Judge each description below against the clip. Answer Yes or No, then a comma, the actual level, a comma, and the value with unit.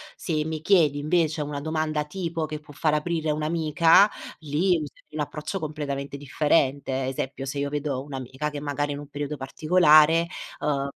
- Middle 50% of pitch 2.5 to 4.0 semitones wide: No, narrow, 1.8 semitones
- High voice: No, medium, 150 Hz